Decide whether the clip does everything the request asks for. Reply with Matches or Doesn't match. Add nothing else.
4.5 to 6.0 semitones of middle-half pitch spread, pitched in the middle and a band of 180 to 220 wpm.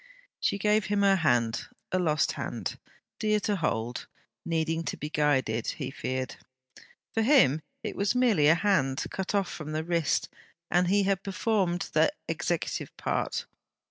Doesn't match